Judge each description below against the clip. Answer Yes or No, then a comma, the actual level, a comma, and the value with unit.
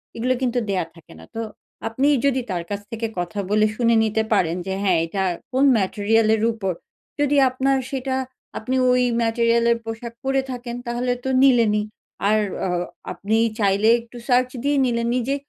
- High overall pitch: Yes, high, 230 Hz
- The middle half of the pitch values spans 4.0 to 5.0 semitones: No, average, 3.3 semitones